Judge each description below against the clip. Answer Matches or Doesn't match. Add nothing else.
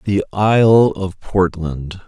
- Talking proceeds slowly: Matches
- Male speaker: Matches